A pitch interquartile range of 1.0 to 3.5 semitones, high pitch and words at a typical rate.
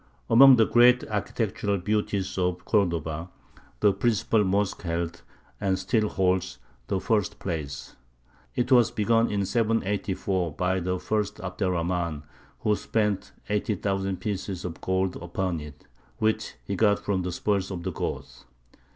No: average, 2.8 semitones; very low, 95 Hz; average, 145 wpm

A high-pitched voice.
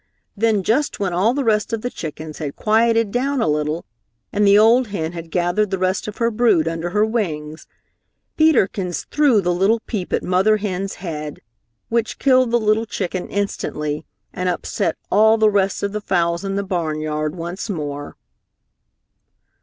Yes: high, 195 Hz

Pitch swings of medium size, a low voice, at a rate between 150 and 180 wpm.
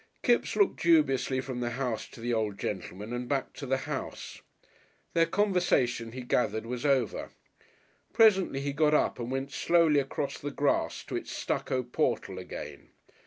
Yes: average, 3.7 semitones; low, 130 Hz; average, 165 wpm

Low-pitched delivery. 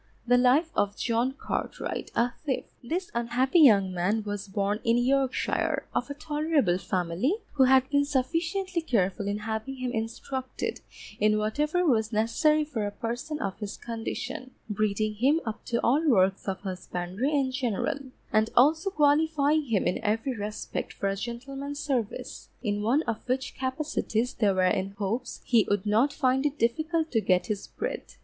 No: high, 245 Hz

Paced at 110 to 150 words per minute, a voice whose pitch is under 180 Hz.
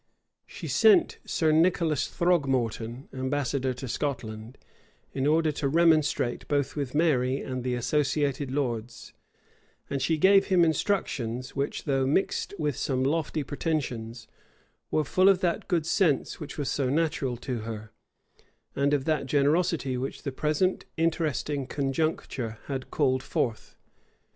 Yes: slow, 135 wpm; medium, 140 Hz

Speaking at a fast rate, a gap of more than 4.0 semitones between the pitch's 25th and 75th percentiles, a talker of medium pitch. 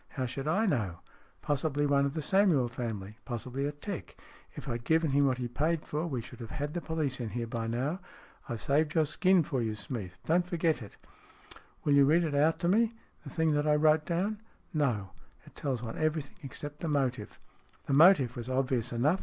Yes: fast, 235 wpm; average, 4.7 semitones; medium, 145 Hz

